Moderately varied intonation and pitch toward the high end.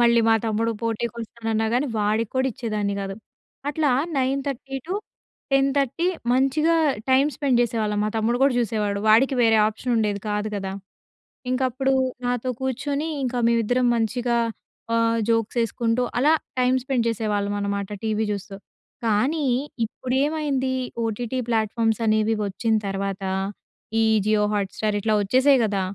Yes: average, 3.4 semitones; high, 230 Hz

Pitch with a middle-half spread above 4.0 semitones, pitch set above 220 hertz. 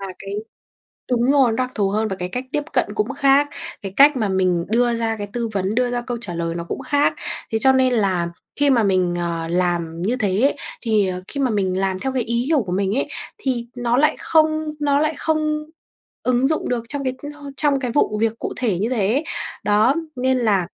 Yes: wide, 5.6 semitones; high, 235 Hz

